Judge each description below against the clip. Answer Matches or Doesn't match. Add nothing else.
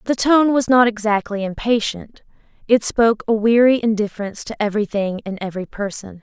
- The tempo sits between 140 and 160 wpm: Matches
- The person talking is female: Matches